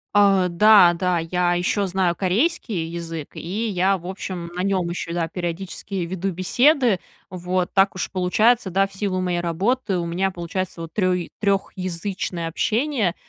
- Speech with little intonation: Yes, narrow, 2.3 semitones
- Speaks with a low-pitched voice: No, medium, 185 Hz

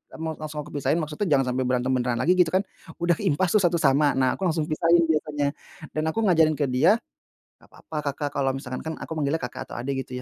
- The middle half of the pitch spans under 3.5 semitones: No, average, 3.8 semitones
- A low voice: No, medium, 150 Hz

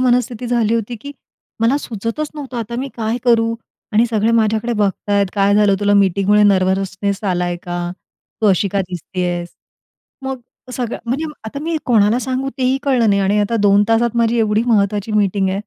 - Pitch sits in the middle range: No, high, 215 Hz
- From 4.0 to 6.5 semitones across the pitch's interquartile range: No, average, 3.1 semitones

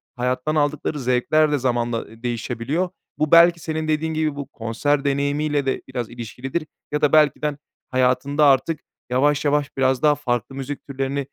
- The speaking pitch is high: No, medium, 140 Hz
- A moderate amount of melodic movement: Yes, average, 3.0 semitones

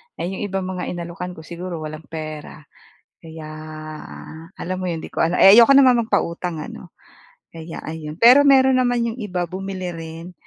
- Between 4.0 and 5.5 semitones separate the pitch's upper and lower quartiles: Yes, average, 5.1 semitones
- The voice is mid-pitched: Yes, medium, 180 Hz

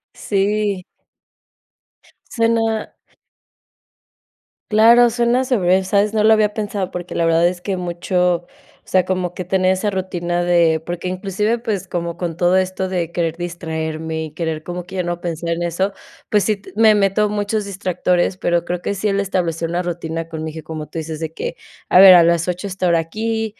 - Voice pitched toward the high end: No, medium, 180 Hz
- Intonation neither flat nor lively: Yes, average, 3.0 semitones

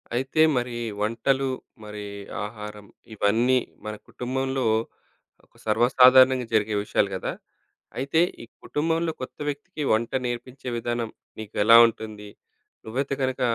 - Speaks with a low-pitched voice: Yes, low, 120 Hz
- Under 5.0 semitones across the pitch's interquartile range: Yes, average, 3.5 semitones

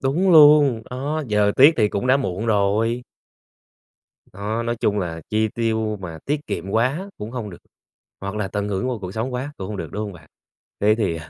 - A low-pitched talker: Yes, low, 110 Hz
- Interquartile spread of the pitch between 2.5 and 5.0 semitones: Yes, average, 4.1 semitones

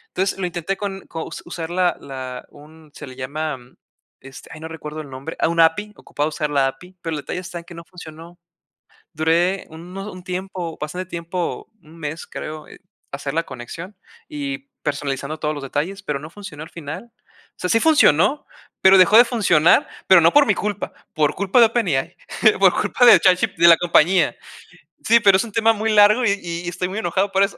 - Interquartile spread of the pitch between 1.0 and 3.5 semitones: No, average, 4.2 semitones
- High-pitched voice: No, medium, 170 Hz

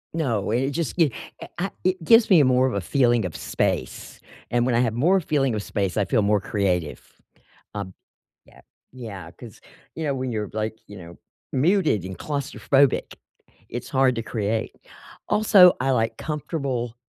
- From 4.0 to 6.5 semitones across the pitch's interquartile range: Yes, wide, 5.5 semitones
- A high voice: No, low, 120 Hz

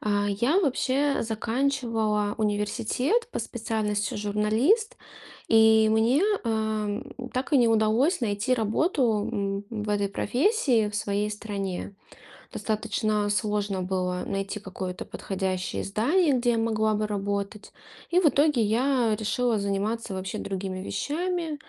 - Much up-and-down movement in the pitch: No, average, 3.4 semitones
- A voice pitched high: Yes, high, 215 Hz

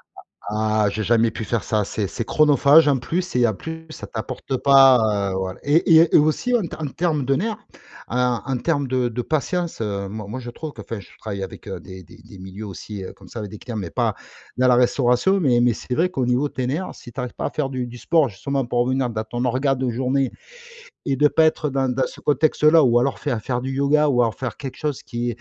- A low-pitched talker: Yes, low, 125 Hz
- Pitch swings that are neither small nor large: Yes, average, 4.2 semitones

